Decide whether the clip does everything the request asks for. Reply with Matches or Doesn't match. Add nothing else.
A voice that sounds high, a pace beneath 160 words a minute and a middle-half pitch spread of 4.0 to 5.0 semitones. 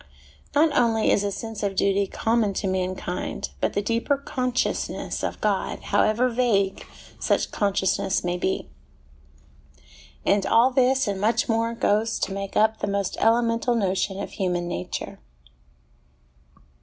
Doesn't match